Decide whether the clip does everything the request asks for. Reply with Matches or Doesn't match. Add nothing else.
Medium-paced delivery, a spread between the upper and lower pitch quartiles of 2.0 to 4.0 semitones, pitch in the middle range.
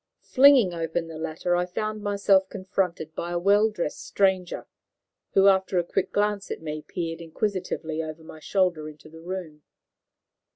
Matches